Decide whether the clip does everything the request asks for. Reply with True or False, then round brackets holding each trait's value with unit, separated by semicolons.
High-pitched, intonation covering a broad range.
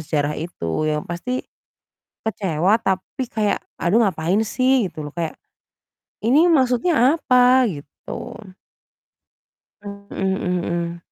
True (195 Hz; 6.7 semitones)